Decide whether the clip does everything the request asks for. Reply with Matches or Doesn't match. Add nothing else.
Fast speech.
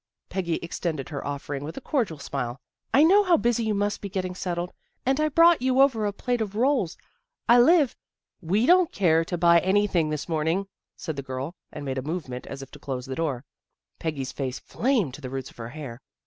Matches